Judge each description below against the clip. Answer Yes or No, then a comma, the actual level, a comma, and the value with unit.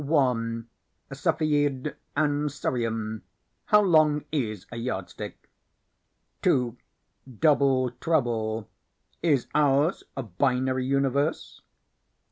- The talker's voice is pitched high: No, low, 135 Hz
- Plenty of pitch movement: No, average, 3.9 semitones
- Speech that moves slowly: Yes, slow, 80 wpm